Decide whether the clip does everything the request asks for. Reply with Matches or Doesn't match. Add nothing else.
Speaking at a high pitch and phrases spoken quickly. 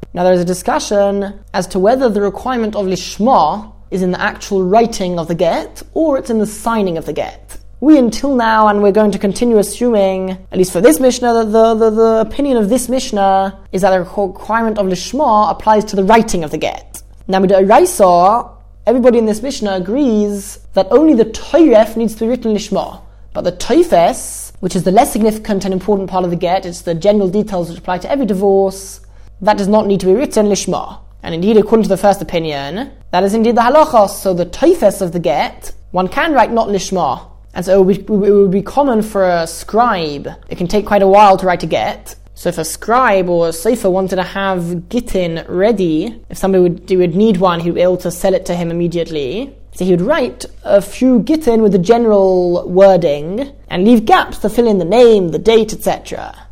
Matches